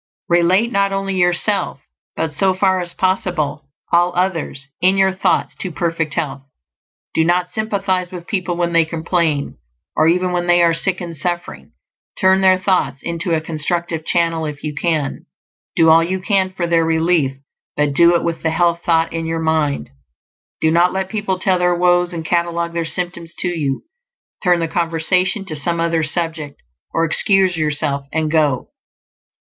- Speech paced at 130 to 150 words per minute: No, average, 175 wpm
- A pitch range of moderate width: No, narrow, 2.1 semitones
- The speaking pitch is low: No, medium, 170 Hz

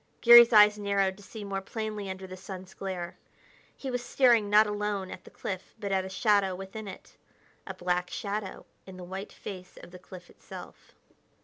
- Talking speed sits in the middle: Yes, average, 190 wpm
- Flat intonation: Yes, narrow, 2.0 semitones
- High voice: Yes, high, 195 Hz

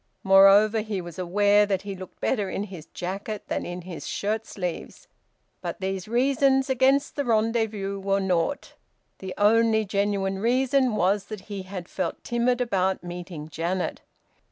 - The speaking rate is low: No, average, 155 wpm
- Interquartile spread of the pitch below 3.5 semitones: Yes, average, 3.1 semitones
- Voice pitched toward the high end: Yes, high, 200 Hz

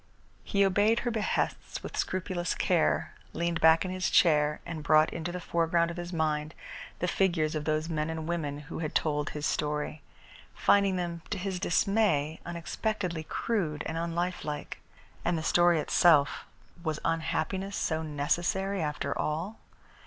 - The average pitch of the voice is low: No, medium, 165 Hz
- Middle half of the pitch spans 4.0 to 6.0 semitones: No, average, 3.0 semitones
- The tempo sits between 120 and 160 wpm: Yes, average, 150 wpm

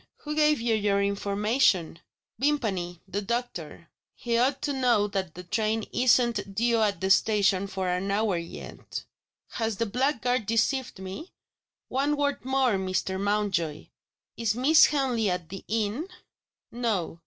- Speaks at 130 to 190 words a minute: Yes, average, 140 wpm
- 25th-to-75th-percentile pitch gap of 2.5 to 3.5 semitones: No, average, 4.3 semitones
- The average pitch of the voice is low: No, high, 215 Hz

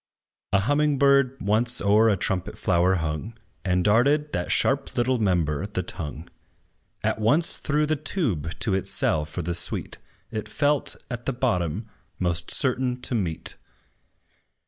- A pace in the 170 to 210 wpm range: No, average, 150 wpm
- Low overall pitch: Yes, low, 110 Hz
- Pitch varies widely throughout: Yes, wide, 7.0 semitones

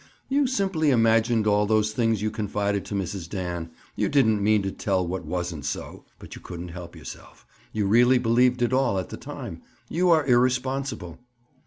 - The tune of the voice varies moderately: Yes, average, 4.7 semitones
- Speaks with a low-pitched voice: Yes, low, 110 Hz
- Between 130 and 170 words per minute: No, average, 180 wpm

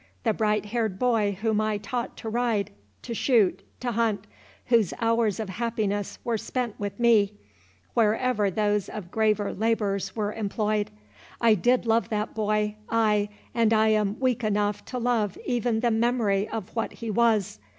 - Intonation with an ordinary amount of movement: No, narrow, 2.0 semitones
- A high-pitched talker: Yes, high, 215 Hz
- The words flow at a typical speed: Yes, average, 150 wpm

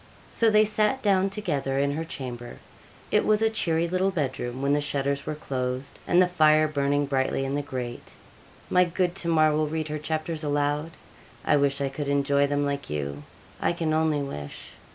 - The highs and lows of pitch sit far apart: No, average, 3.2 semitones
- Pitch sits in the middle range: Yes, medium, 145 Hz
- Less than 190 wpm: No, average, 195 wpm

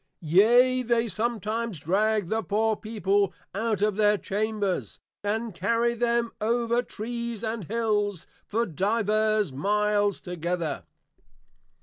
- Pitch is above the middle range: Yes, high, 215 Hz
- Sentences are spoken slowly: Yes, slow, 110 wpm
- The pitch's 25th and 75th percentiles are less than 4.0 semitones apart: Yes, narrow, 2.5 semitones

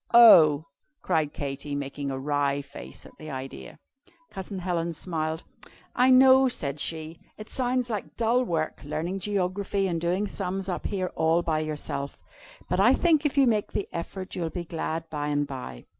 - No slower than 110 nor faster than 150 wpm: No, average, 175 wpm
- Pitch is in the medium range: Yes, medium, 170 Hz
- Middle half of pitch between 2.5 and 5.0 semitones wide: No, wide, 5.4 semitones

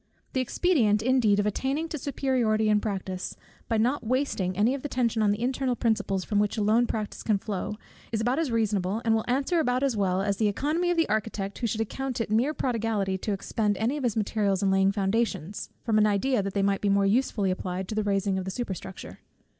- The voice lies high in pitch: Yes, high, 215 Hz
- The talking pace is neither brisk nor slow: No, fast, 225 wpm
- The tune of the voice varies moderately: Yes, average, 3.8 semitones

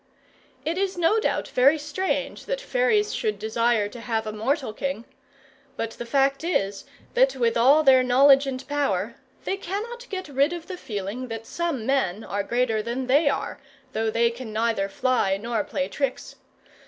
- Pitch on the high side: Yes, very high, 260 Hz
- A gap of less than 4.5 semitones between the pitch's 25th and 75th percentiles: No, average, 5.3 semitones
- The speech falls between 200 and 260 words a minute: No, average, 175 wpm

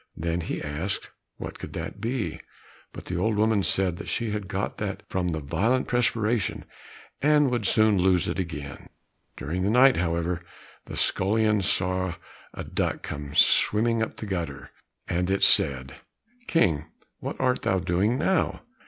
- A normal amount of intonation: Yes, average, 4.6 semitones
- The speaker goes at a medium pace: Yes, average, 160 wpm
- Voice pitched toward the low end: Yes, very low, 95 Hz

